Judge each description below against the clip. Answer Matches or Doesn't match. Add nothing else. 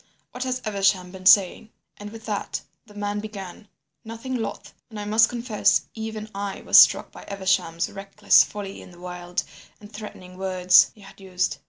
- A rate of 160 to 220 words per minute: Matches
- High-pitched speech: Matches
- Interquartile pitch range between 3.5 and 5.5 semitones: Doesn't match